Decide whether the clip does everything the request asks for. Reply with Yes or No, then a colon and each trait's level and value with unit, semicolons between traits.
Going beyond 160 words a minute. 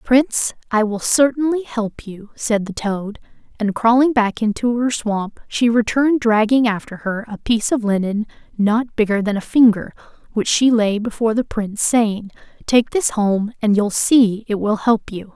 Yes: average, 180 wpm